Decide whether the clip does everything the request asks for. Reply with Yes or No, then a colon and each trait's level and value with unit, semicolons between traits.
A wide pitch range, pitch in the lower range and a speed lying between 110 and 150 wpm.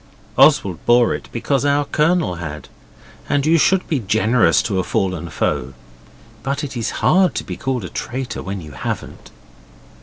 No: wide, 7.7 semitones; low, 120 Hz; average, 170 wpm